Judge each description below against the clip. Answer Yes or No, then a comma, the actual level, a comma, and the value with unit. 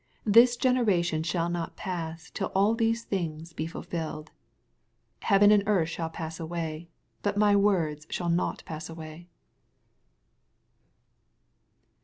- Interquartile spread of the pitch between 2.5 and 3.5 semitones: No, average, 4.0 semitones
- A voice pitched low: No, medium, 170 Hz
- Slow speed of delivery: Yes, slow, 130 wpm